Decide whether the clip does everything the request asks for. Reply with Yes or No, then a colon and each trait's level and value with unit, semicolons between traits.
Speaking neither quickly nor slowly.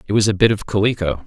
No: fast, 285 wpm